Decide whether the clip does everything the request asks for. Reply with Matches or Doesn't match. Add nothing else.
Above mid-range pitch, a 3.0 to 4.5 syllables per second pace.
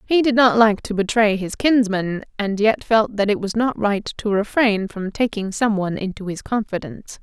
Doesn't match